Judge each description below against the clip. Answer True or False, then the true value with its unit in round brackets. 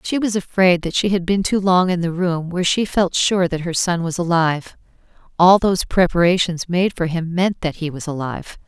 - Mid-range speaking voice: True (175 Hz)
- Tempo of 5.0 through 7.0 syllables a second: True (5.3 syllables/s)